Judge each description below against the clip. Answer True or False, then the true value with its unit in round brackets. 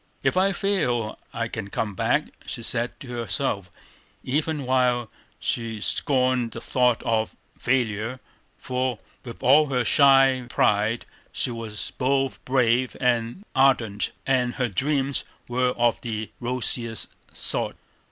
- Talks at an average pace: False (130 wpm)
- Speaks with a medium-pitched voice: False (125 Hz)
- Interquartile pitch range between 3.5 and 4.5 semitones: False (2.5 semitones)